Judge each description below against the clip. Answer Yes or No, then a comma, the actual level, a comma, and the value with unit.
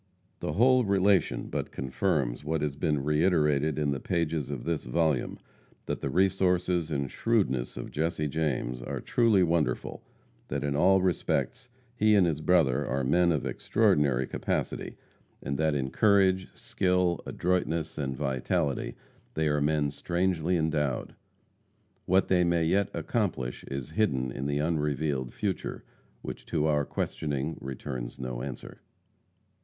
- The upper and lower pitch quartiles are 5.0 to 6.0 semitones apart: No, average, 4.5 semitones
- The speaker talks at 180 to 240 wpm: No, average, 140 wpm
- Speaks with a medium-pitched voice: No, very low, 80 Hz